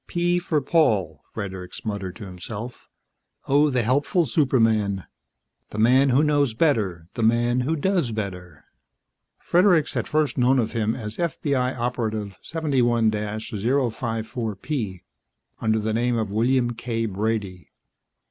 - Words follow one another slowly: Yes, slow, 130 wpm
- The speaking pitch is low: Yes, low, 115 Hz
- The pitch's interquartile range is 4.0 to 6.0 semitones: Yes, average, 4.3 semitones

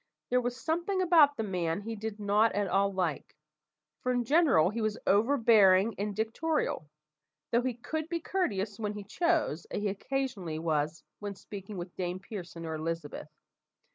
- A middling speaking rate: Yes, average, 170 wpm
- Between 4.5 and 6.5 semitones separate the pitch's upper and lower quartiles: Yes, average, 5.1 semitones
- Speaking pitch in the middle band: No, high, 210 Hz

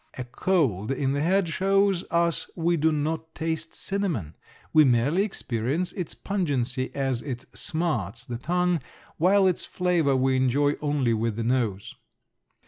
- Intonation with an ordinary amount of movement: No, wide, 5.7 semitones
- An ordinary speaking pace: Yes, average, 145 wpm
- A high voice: No, medium, 145 Hz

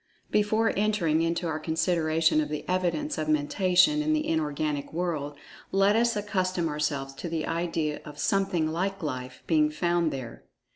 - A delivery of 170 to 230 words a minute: No, average, 155 wpm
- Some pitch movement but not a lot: Yes, average, 3.4 semitones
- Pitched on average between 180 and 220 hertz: No, medium, 165 Hz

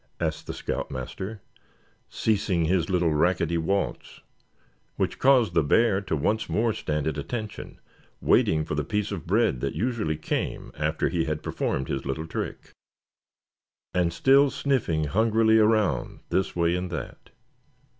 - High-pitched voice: No, very low, 90 Hz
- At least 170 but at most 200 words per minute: No, average, 145 wpm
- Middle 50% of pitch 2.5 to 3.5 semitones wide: No, wide, 5.6 semitones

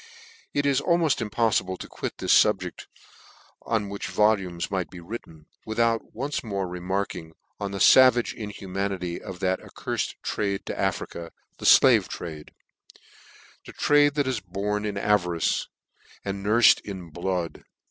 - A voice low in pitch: Yes, low, 100 Hz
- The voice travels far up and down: No, average, 3.9 semitones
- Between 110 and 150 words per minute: Yes, average, 145 wpm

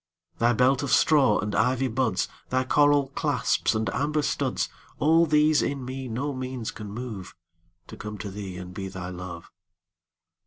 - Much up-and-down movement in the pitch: Yes, wide, 5.7 semitones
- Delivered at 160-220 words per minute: No, average, 150 wpm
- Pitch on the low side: Yes, low, 120 Hz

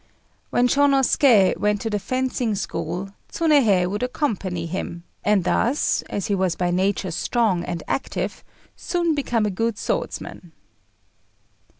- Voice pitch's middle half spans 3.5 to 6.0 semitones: Yes, wide, 5.4 semitones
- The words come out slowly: Yes, slow, 130 wpm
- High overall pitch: Yes, high, 210 Hz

